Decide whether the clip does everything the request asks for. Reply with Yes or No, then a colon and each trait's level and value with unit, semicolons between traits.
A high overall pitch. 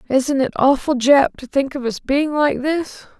Yes: very high, 275 Hz